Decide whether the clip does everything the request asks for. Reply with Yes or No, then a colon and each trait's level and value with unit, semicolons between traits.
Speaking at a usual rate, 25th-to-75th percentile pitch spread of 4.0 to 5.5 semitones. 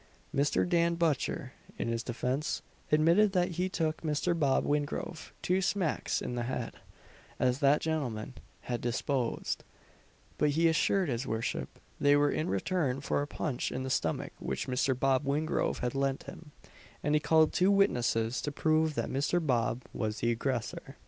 Yes: average, 165 wpm; average, 4.3 semitones